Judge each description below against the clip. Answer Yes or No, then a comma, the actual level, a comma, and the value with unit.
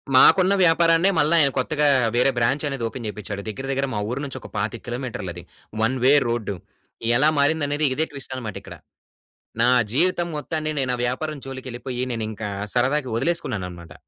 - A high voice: No, low, 130 Hz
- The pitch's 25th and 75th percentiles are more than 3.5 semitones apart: Yes, average, 4.4 semitones